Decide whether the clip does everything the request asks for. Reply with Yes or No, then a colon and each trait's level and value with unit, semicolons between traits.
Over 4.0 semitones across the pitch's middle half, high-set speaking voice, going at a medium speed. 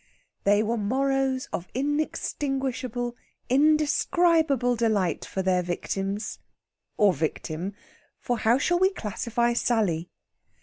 No: average, 5.1 semitones; high, 240 Hz; slow, 100 wpm